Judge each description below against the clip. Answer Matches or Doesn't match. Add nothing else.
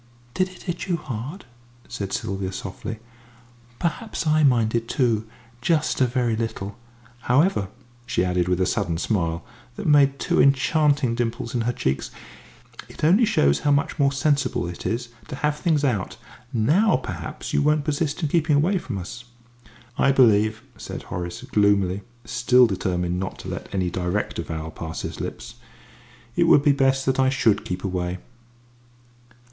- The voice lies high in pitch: Doesn't match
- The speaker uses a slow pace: Doesn't match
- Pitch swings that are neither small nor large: Doesn't match